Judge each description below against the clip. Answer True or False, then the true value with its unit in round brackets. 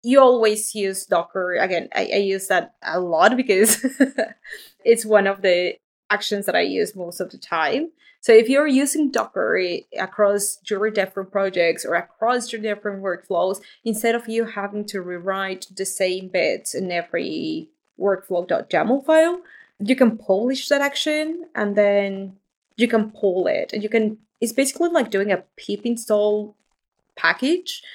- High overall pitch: True (210 Hz)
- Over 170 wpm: False (155 wpm)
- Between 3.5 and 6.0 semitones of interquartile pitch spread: True (4.7 semitones)